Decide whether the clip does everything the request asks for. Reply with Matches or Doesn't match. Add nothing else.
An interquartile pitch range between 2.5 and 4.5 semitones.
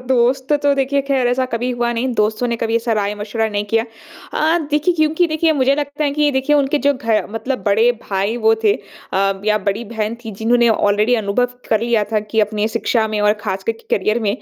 Matches